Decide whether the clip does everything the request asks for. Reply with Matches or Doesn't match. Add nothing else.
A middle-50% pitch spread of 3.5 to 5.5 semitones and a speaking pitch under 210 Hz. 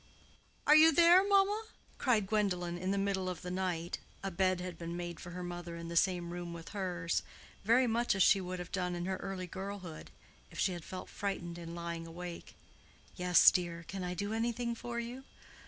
Doesn't match